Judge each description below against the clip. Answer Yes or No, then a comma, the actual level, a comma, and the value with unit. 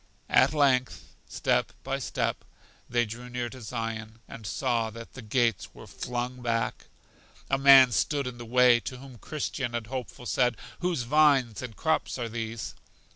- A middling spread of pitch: No, narrow, 2.3 semitones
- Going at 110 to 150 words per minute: No, average, 165 wpm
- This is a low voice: Yes, low, 120 Hz